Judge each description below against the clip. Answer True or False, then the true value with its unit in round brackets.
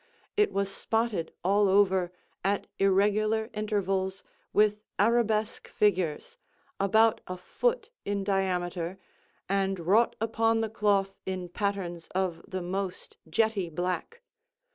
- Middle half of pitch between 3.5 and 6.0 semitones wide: False (2.5 semitones)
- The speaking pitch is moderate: False (195 Hz)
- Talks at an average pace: False (115 wpm)